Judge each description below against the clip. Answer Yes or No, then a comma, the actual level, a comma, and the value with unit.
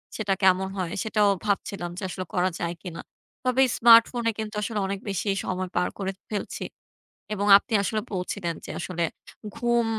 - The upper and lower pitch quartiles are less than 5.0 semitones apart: Yes, average, 3.0 semitones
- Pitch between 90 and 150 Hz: No, high, 200 Hz